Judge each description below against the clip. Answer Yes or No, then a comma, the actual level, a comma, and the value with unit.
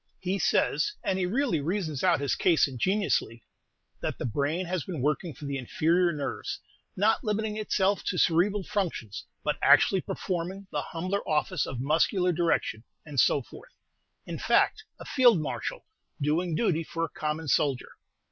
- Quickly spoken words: No, average, 160 wpm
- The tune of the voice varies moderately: Yes, average, 4.4 semitones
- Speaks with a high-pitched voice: No, medium, 170 Hz